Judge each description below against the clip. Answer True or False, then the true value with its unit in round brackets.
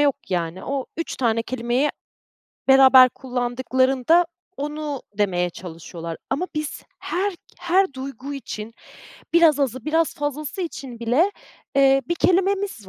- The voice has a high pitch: True (270 Hz)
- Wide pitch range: False (4.2 semitones)